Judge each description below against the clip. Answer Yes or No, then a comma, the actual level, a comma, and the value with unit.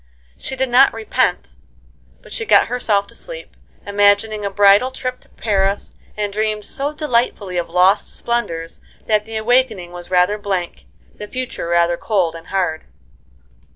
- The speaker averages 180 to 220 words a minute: No, average, 155 wpm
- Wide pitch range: No, average, 4.5 semitones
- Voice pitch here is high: Yes, high, 205 Hz